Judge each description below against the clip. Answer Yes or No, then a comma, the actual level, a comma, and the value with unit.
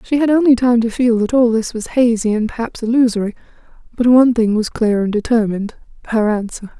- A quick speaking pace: No, average, 195 wpm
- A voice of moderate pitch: No, high, 230 Hz